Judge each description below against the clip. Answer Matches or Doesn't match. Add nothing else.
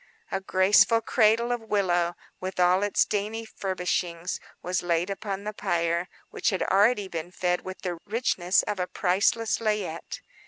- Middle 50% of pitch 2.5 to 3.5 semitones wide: Matches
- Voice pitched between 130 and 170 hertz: Doesn't match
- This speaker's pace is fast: Doesn't match